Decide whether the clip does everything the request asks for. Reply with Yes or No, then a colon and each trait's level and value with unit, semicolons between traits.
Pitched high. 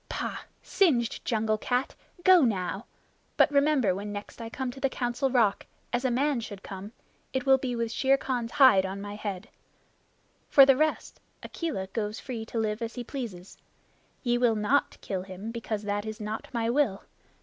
Yes: high, 230 Hz